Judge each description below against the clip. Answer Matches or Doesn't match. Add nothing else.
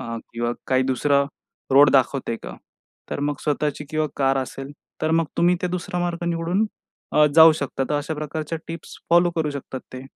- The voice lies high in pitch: Doesn't match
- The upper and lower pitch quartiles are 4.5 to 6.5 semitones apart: Doesn't match